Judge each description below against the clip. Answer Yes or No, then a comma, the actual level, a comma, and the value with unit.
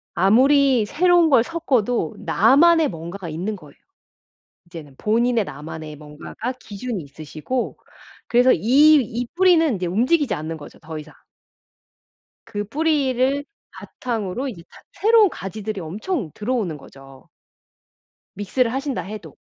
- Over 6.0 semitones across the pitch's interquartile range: Yes, wide, 8.1 semitones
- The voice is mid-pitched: No, high, 220 Hz